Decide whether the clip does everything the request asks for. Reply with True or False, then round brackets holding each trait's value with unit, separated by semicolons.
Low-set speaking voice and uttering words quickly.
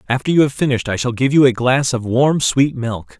True (130 Hz; 265 wpm)